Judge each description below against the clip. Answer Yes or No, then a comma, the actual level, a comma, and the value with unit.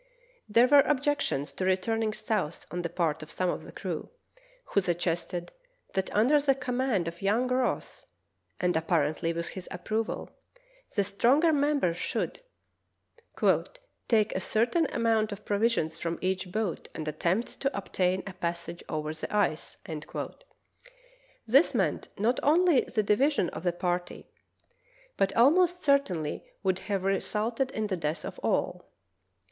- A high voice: Yes, high, 200 Hz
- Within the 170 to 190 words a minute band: No, average, 150 wpm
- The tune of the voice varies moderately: No, wide, 6.1 semitones